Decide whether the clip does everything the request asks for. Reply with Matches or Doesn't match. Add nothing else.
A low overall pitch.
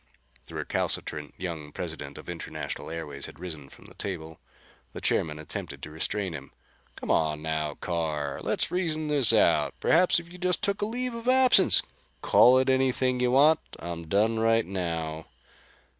Matches